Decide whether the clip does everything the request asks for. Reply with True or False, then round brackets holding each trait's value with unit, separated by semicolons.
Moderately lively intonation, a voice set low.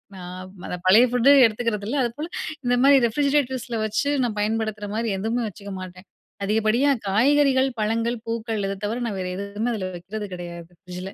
False (3.3 semitones; 220 Hz)